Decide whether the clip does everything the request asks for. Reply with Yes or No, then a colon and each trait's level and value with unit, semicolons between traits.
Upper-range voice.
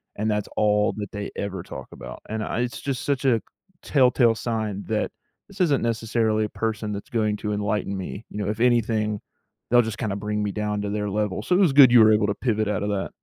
No: low, 110 Hz